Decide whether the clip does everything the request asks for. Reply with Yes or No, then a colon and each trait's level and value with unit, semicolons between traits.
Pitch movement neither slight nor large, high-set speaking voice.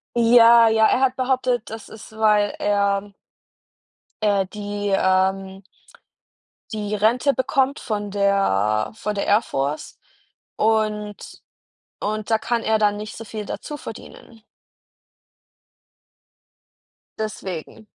No: narrow, 2.1 semitones; high, 210 Hz